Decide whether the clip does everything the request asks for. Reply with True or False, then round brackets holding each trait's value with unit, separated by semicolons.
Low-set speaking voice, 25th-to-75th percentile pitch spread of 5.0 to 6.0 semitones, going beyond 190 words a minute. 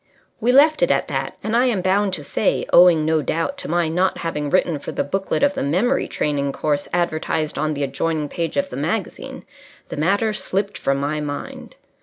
False (170 Hz; 5.3 semitones; 205 wpm)